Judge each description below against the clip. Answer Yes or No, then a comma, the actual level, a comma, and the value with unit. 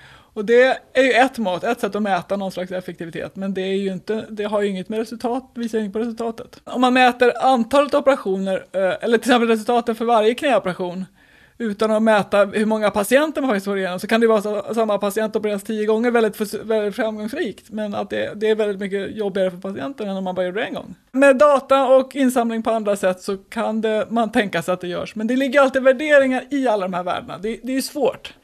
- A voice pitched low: No, high, 220 Hz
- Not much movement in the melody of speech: No, average, 3.5 semitones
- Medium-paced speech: No, fast, 240 wpm